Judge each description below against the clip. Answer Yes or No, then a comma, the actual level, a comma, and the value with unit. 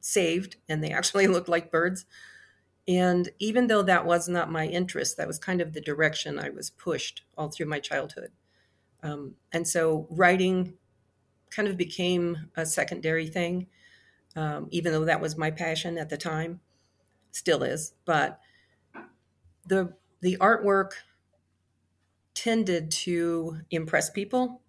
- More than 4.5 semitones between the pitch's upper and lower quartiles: No, average, 3.2 semitones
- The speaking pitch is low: No, medium, 170 Hz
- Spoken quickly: No, average, 140 wpm